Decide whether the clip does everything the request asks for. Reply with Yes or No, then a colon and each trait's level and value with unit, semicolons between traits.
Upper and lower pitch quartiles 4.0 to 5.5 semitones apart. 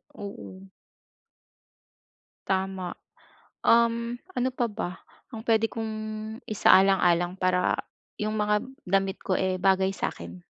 No: average, 2.9 semitones